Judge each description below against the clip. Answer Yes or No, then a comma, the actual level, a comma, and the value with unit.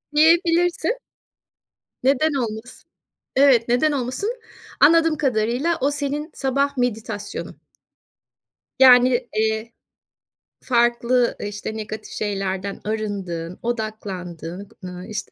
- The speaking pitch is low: No, high, 240 Hz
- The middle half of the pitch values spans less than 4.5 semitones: No, average, 4.9 semitones